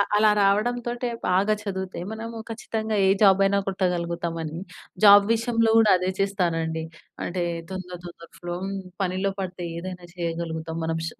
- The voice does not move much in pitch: No, average, 3.5 semitones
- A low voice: No, high, 190 Hz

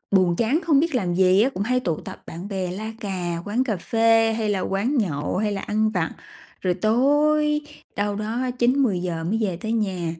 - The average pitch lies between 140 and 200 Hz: No, high, 210 Hz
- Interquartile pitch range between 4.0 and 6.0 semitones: Yes, average, 4.6 semitones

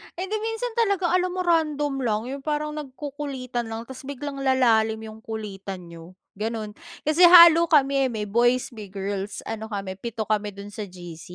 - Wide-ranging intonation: Yes, wide, 6.0 semitones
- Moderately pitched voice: No, high, 240 Hz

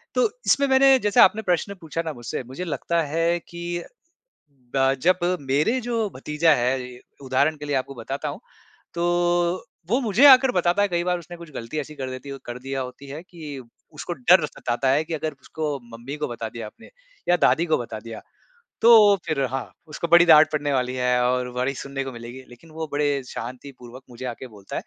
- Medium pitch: Yes, medium, 145 Hz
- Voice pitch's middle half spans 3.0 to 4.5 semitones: No, average, 5.1 semitones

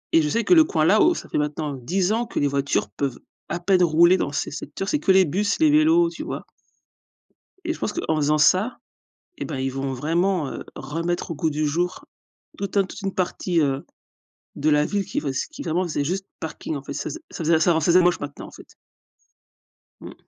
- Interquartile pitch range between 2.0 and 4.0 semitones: No, average, 4.7 semitones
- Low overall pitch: No, medium, 170 Hz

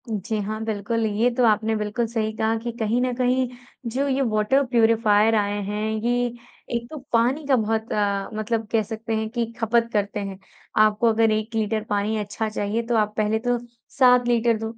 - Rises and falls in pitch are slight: Yes, narrow, 1.9 semitones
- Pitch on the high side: Yes, high, 220 Hz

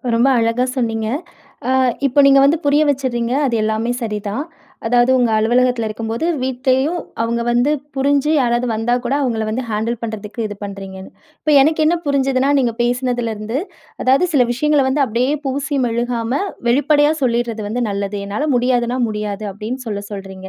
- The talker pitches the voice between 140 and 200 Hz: No, high, 240 Hz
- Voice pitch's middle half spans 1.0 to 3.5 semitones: Yes, average, 3.2 semitones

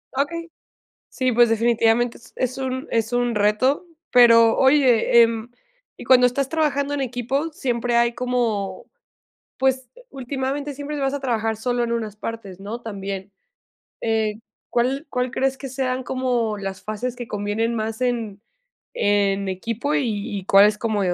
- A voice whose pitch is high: Yes, high, 240 Hz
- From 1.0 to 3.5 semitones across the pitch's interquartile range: Yes, average, 3.2 semitones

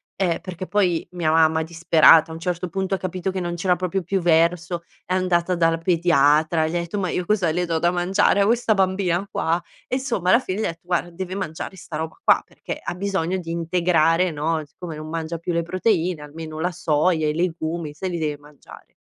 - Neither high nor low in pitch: Yes, medium, 175 Hz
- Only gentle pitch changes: Yes, narrow, 2.2 semitones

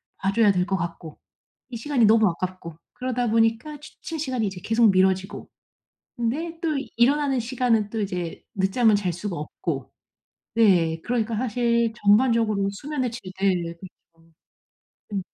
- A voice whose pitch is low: No, high, 220 Hz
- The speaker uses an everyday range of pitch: Yes, average, 4.4 semitones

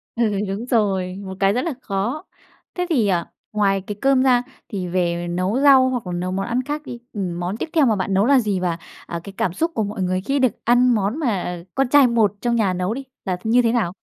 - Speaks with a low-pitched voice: No, high, 210 Hz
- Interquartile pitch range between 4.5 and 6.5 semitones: Yes, average, 5.1 semitones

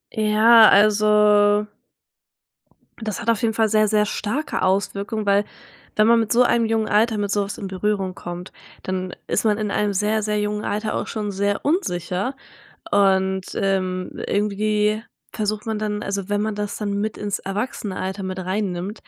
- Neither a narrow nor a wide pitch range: No, narrow, 1.5 semitones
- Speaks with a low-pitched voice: No, high, 210 Hz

